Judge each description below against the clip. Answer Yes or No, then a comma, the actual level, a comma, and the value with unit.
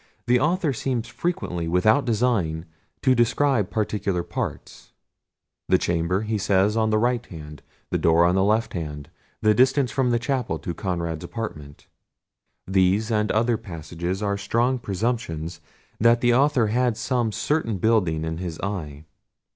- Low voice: Yes, low, 105 Hz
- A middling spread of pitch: No, wide, 5.7 semitones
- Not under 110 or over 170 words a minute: Yes, average, 150 wpm